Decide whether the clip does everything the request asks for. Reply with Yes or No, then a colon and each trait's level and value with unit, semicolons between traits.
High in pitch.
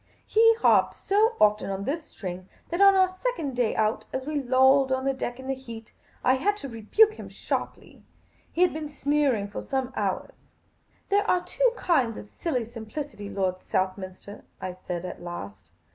Yes: very high, 260 Hz